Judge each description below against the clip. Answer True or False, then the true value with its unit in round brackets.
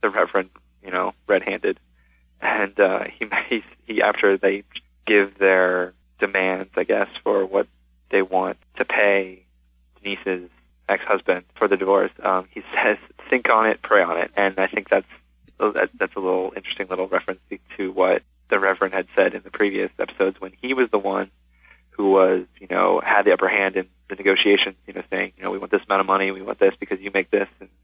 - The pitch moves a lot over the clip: True (8.2 semitones)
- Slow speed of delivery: False (205 wpm)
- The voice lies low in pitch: True (95 Hz)